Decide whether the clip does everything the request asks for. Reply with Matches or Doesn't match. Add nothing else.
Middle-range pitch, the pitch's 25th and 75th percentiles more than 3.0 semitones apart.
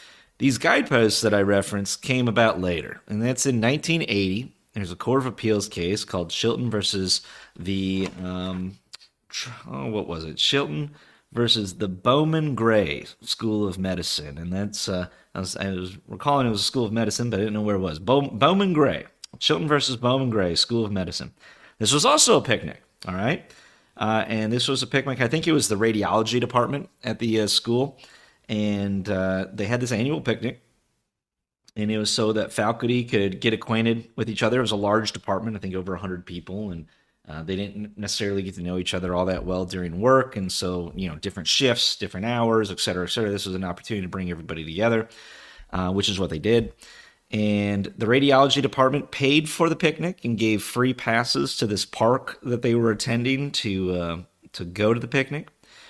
Doesn't match